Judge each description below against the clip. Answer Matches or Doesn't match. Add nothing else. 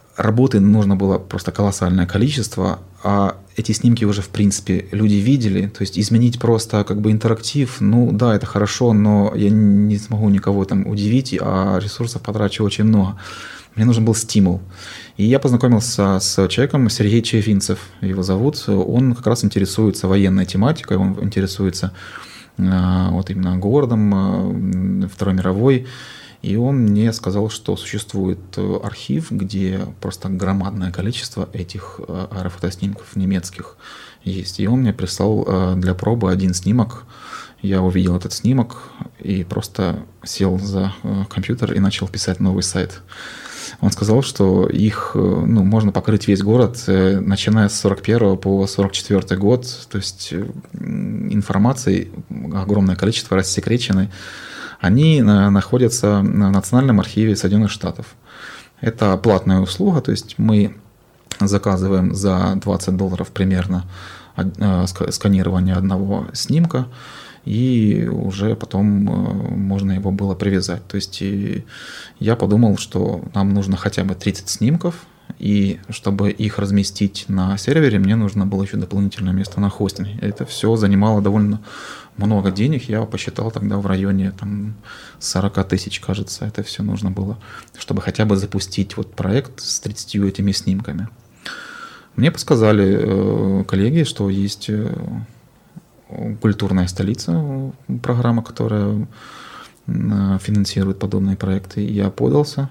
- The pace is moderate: Matches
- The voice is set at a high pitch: Doesn't match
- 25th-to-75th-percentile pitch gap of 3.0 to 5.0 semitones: Doesn't match